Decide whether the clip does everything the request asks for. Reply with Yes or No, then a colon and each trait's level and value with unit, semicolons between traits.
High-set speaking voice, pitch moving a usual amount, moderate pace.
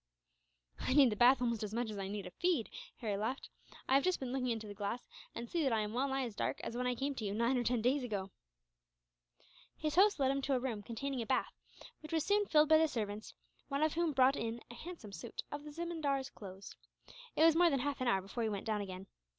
No: very high, 250 Hz; average, 4.8 semitones; fast, 260 wpm